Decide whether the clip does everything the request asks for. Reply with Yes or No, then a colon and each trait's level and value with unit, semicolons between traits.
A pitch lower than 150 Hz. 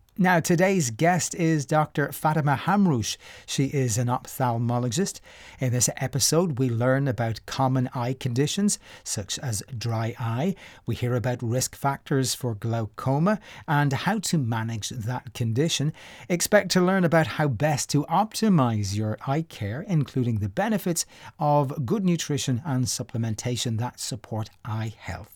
Yes: low, 135 Hz